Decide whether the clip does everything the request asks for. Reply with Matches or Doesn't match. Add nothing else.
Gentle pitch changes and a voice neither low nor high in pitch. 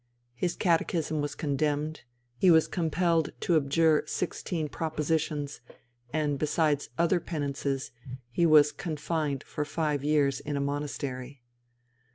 Matches